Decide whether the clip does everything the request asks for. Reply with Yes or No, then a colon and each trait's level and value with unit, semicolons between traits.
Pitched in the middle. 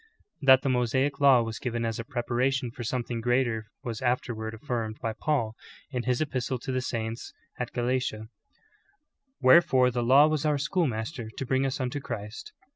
No: low, 125 Hz